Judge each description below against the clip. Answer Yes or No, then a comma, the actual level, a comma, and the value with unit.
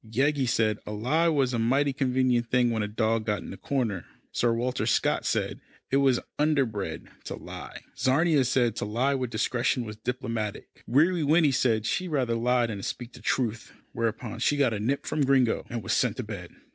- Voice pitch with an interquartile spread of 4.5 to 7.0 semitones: No, average, 3.4 semitones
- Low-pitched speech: Yes, low, 125 Hz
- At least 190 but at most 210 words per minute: Yes, average, 195 wpm